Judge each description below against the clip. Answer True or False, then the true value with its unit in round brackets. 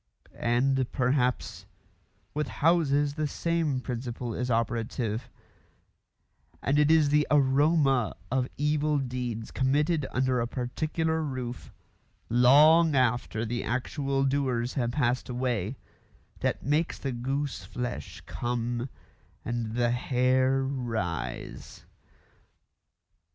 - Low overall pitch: True (130 Hz)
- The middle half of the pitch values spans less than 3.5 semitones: True (3.1 semitones)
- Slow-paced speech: True (100 wpm)